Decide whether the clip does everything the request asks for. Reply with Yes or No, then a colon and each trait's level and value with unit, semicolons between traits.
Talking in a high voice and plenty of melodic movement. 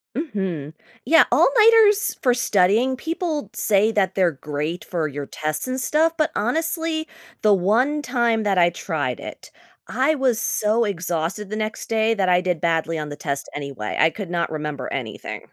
Yes: high, 205 Hz; wide, 8.0 semitones